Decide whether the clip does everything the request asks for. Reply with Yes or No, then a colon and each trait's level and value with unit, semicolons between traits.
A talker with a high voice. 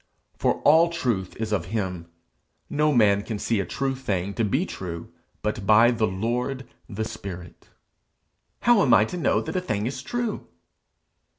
No: low, 110 Hz